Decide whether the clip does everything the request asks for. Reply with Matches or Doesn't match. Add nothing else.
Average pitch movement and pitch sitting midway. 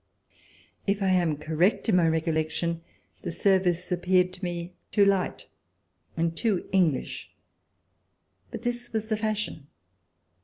Matches